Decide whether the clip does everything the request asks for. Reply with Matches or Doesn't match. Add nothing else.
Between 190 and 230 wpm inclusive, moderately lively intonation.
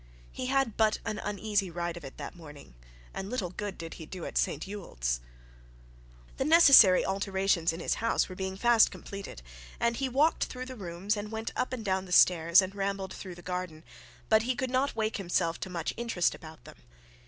Matches